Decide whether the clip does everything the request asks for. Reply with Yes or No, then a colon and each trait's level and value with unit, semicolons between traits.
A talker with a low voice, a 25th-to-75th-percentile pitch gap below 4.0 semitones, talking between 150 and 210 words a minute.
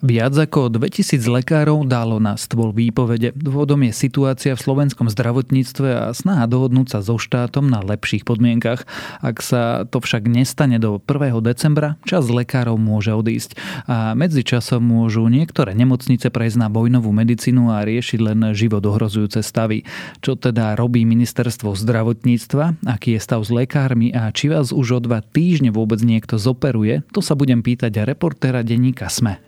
Yes: low, 120 Hz; average, 2.8 semitones; average, 160 wpm